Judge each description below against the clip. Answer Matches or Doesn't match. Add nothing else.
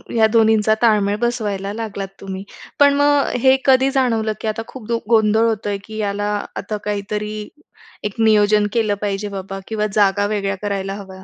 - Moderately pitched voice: Doesn't match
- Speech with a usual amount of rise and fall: Doesn't match